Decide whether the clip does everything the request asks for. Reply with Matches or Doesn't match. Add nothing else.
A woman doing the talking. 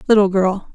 Matches